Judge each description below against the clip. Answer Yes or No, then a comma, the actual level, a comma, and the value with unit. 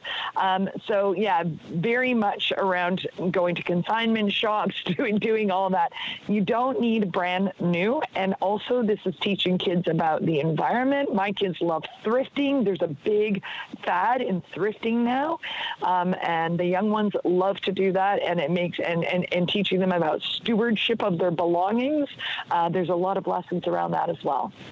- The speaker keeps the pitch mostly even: No, average, 3.8 semitones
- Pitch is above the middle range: Yes, high, 195 Hz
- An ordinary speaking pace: Yes, average, 170 wpm